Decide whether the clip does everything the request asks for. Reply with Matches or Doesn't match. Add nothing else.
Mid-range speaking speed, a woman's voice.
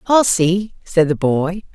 Matches